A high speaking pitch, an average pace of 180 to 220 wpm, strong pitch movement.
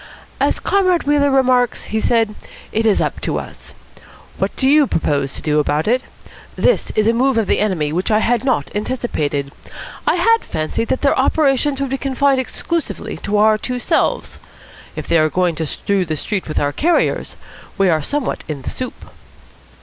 Yes: high, 225 Hz; average, 190 wpm; wide, 8.3 semitones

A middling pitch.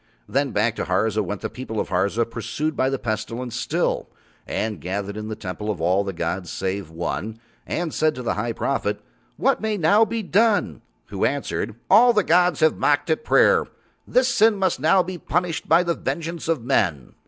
No: low, 130 Hz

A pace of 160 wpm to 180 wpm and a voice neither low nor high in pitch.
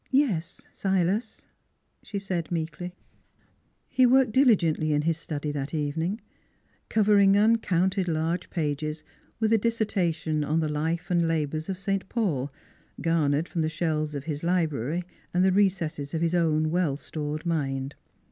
No: average, 145 wpm; medium, 165 Hz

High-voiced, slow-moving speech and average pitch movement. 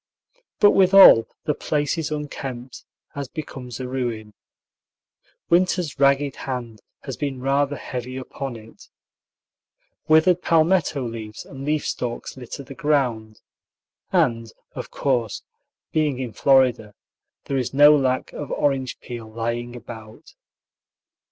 No: low, 135 Hz; slow, 120 wpm; average, 3.6 semitones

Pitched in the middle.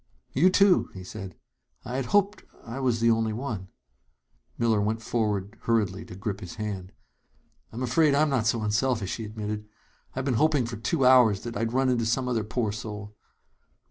No: low, 115 Hz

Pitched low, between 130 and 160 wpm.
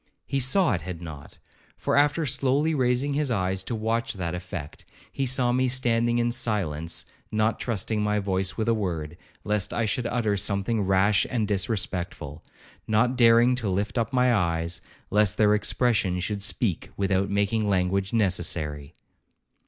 Yes: low, 105 Hz; average, 155 wpm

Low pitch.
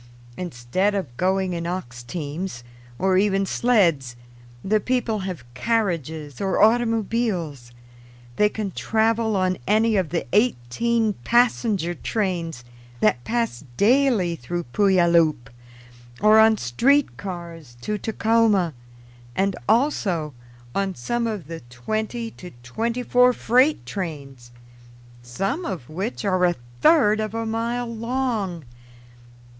No: high, 195 Hz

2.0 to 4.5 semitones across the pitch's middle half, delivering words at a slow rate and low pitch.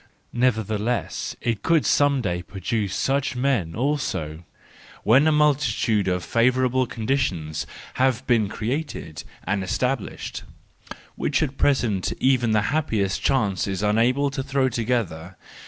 No: average, 5.1 semitones; slow, 120 wpm; low, 120 Hz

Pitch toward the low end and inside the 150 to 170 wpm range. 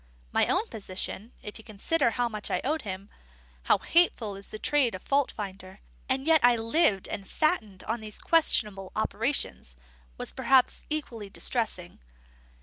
No: high, 225 Hz; average, 160 wpm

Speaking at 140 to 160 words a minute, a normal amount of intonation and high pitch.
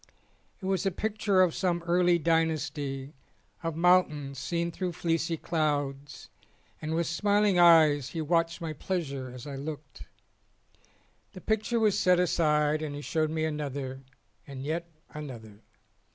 No: average, 145 wpm; average, 3.3 semitones; medium, 160 Hz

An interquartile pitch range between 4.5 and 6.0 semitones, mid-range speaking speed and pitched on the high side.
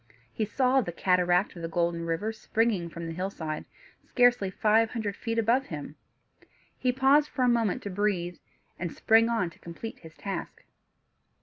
Yes: average, 5.0 semitones; average, 170 wpm; high, 205 Hz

